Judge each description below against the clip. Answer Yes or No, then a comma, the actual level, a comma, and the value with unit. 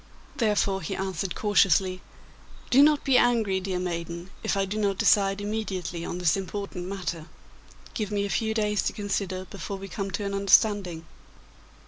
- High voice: Yes, high, 195 Hz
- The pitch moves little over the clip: Yes, narrow, 2.2 semitones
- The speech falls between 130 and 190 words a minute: Yes, average, 165 wpm